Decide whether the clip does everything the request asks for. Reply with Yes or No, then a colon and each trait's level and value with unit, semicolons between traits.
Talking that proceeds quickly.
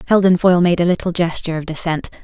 Yes: fast, 215 wpm